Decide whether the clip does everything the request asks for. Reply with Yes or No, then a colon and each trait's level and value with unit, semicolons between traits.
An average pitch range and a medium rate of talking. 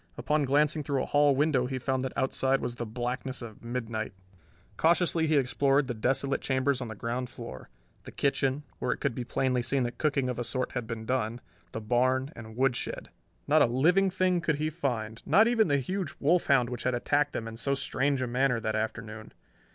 No: average, 3.1 semitones; fast, 210 wpm